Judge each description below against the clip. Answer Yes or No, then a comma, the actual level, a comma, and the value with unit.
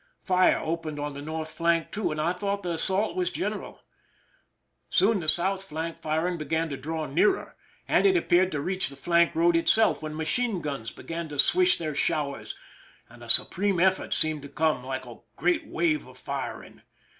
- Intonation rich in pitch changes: No, average, 3.5 semitones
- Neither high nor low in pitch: Yes, medium, 165 Hz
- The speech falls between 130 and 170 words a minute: No, average, 190 wpm